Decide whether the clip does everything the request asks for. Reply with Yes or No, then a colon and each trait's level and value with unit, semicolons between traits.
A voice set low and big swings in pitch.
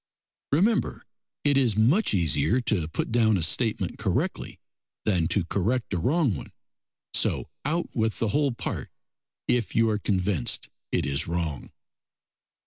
Yes: low, 110 Hz; wide, 6.4 semitones